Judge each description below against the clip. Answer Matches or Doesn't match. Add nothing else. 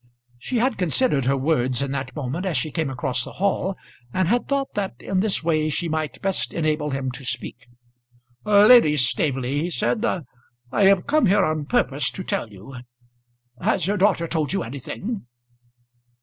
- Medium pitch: Matches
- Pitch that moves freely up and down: Matches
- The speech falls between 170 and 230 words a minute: Matches